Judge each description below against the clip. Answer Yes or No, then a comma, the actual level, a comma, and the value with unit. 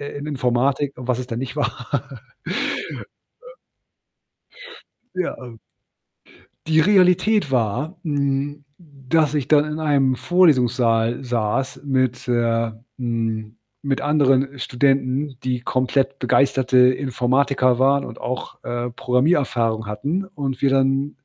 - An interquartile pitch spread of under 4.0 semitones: Yes, average, 2.7 semitones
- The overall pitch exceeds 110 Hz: Yes, low, 135 Hz